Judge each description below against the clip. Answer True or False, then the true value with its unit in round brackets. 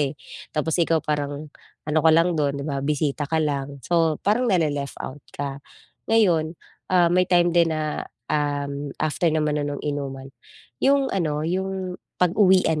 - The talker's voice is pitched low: False (155 Hz)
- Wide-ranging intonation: False (3.4 semitones)